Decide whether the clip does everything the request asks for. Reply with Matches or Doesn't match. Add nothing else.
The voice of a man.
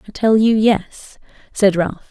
Doesn't match